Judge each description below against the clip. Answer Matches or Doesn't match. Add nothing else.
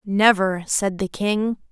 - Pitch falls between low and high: Doesn't match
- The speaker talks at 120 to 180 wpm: Matches